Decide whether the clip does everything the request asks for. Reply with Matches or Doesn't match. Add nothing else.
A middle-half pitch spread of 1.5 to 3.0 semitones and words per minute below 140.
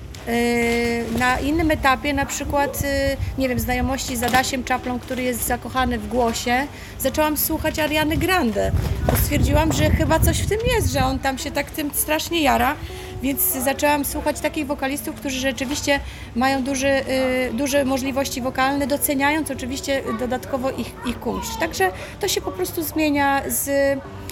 Doesn't match